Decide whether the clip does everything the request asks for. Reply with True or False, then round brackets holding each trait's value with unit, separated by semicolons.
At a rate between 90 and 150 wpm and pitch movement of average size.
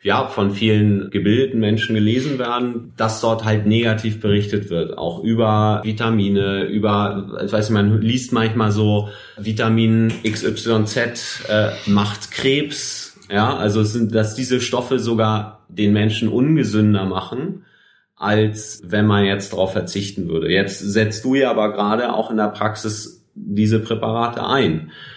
False (140 wpm; 1.5 semitones)